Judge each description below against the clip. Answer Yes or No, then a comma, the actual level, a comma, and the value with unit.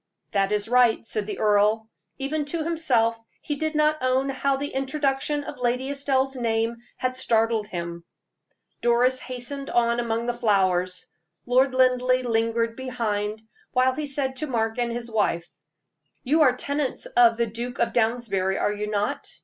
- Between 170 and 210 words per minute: No, average, 160 wpm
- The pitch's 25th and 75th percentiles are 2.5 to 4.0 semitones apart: Yes, average, 3.1 semitones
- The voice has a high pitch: Yes, high, 240 Hz